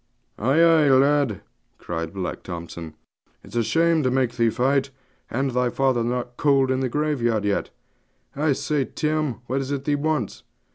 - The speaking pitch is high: No, low, 130 Hz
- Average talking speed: Yes, average, 170 wpm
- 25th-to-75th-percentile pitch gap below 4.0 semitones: Yes, average, 3.5 semitones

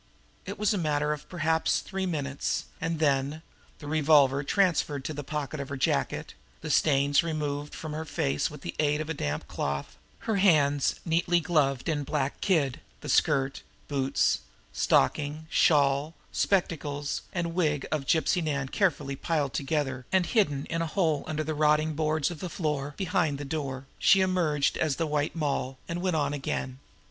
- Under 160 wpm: No, average, 175 wpm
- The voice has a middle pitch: Yes, medium, 150 Hz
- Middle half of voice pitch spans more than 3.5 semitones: No, narrow, 2.6 semitones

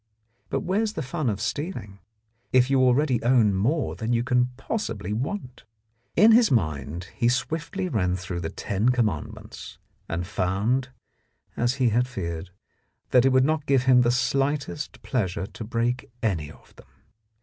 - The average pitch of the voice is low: Yes, low, 125 Hz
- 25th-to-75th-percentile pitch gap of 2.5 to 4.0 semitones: No, average, 5.1 semitones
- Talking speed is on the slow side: No, average, 165 wpm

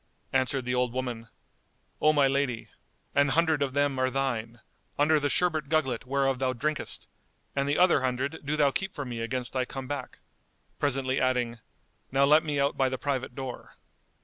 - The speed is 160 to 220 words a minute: Yes, average, 180 wpm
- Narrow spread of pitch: Yes, narrow, 2.0 semitones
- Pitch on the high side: No, low, 135 Hz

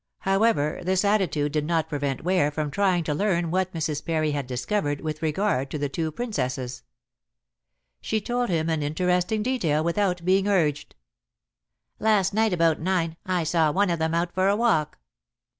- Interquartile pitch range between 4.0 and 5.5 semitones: Yes, average, 4.3 semitones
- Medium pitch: Yes, medium, 170 Hz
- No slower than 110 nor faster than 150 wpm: No, average, 170 wpm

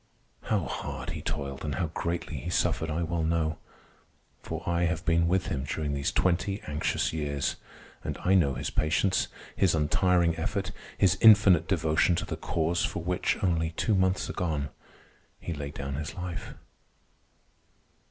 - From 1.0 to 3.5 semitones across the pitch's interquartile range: Yes, average, 2.7 semitones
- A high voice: No, very low, 85 Hz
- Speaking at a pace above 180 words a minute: No, average, 160 wpm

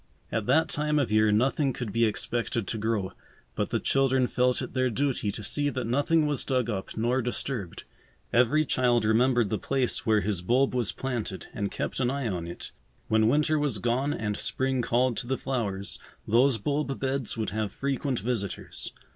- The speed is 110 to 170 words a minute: No, average, 190 wpm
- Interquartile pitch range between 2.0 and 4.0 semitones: Yes, average, 3.7 semitones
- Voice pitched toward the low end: Yes, low, 125 Hz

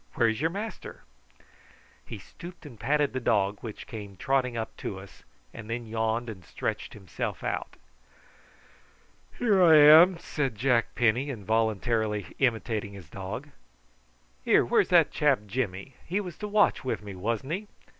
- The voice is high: No, low, 115 Hz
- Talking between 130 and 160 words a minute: Yes, average, 150 wpm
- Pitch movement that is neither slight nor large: No, wide, 5.8 semitones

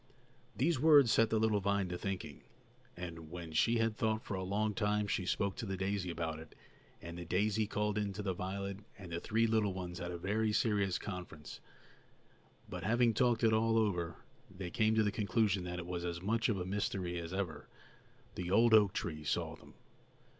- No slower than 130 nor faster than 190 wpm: No, average, 200 wpm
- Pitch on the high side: No, low, 100 Hz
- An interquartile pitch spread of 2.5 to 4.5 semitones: Yes, average, 3.6 semitones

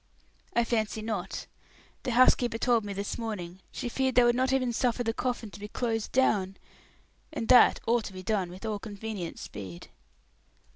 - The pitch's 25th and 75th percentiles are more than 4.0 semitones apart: No, average, 3.3 semitones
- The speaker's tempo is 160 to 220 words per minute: Yes, average, 180 wpm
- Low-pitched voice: No, high, 225 Hz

